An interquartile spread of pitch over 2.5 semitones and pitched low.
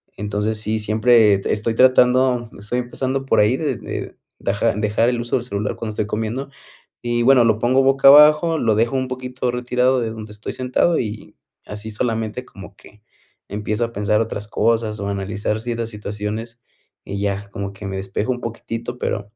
Yes: average, 2.9 semitones; low, 115 Hz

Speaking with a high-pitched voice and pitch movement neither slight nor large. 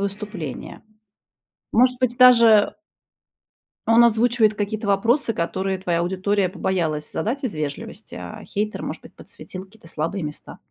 Yes: high, 205 Hz; average, 3.7 semitones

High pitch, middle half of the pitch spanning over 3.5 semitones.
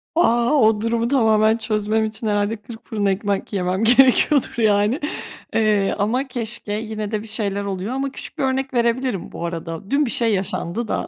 No: high, 220 Hz; average, 2.7 semitones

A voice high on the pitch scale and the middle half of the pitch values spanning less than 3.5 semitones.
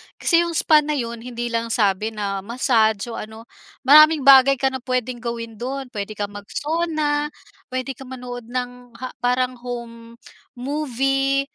Yes: very high, 250 Hz; average, 2.9 semitones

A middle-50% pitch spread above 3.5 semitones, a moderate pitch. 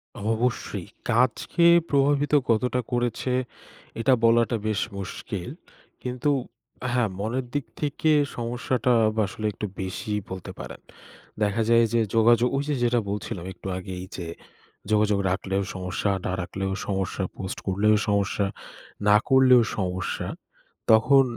No: average, 4.2 semitones; low, 110 Hz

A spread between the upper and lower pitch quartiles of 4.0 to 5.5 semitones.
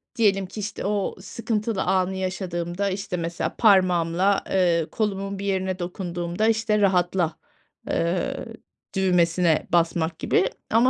No: narrow, 2.4 semitones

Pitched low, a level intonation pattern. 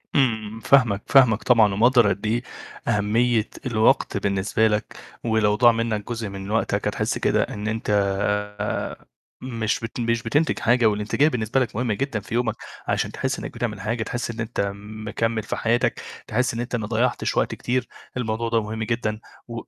Yes: low, 115 Hz; narrow, 2.1 semitones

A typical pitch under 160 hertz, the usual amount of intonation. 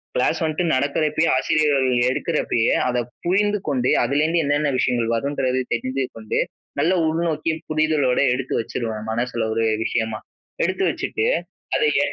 Yes: medium, 140 Hz; average, 4.3 semitones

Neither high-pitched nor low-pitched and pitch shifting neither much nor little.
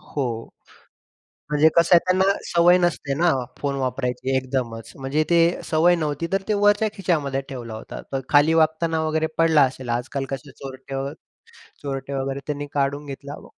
Yes: medium, 145 Hz; average, 3.5 semitones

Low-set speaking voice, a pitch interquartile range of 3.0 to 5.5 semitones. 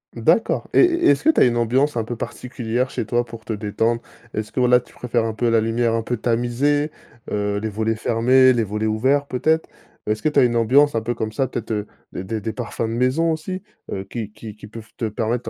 No: low, 115 Hz; narrow, 2.6 semitones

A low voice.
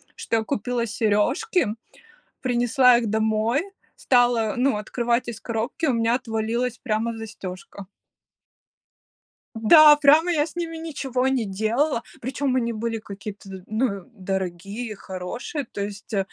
No: high, 230 Hz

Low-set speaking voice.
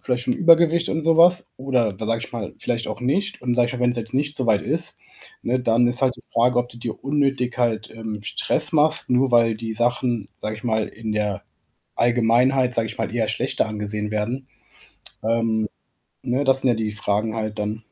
Yes: low, 120 Hz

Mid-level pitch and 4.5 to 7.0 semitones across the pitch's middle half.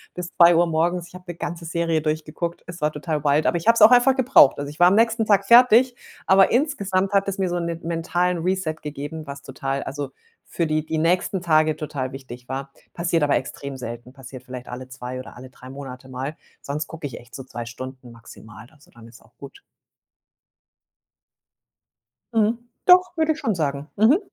Yes: medium, 155 Hz; average, 5.3 semitones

